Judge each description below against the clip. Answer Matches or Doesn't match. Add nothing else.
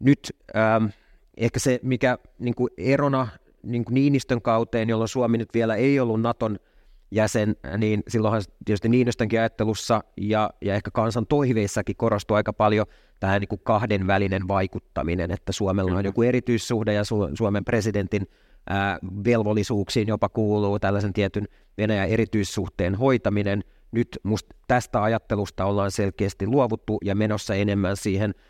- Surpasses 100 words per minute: Matches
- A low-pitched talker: Matches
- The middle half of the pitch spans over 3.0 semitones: Doesn't match